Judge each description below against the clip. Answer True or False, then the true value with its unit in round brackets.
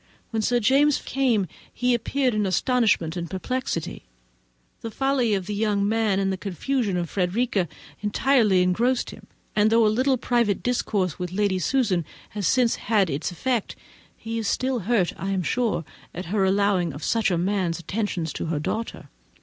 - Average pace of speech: True (175 wpm)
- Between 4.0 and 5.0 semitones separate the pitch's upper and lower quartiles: True (4.5 semitones)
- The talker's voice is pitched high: True (210 Hz)